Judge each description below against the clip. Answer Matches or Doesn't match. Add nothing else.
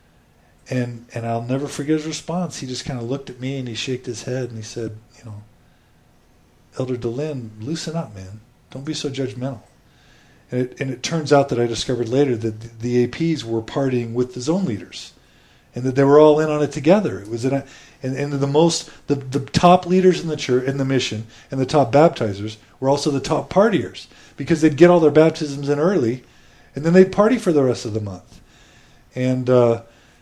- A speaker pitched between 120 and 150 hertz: Matches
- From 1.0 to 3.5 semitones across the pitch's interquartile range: Doesn't match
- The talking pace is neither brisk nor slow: Doesn't match